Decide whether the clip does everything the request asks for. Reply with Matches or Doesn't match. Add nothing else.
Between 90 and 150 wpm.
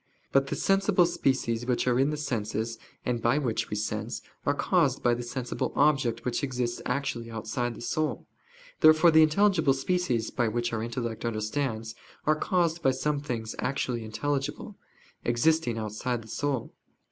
Doesn't match